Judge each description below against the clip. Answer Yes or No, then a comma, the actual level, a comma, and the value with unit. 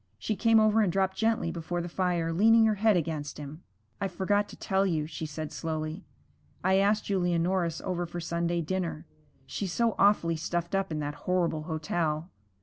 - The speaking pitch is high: No, medium, 175 Hz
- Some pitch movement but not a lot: Yes, average, 3.1 semitones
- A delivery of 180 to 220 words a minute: Yes, average, 185 wpm